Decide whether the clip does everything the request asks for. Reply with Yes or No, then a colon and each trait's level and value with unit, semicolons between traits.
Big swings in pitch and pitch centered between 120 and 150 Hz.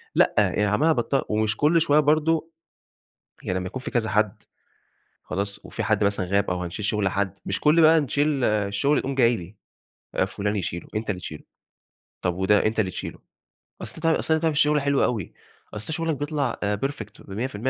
No: wide, 6.6 semitones; low, 110 Hz